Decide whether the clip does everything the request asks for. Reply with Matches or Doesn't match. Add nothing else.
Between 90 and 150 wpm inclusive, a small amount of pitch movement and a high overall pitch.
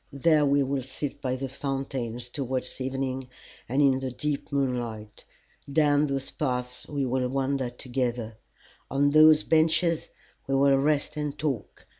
Doesn't match